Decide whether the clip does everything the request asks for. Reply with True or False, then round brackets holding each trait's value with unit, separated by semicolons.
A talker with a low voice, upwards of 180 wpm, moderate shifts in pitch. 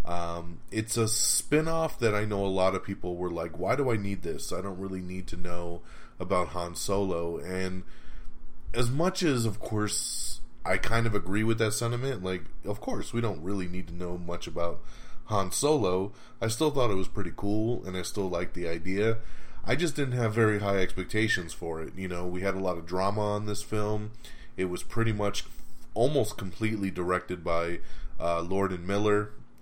True (100 Hz; 200 wpm; 3.9 semitones)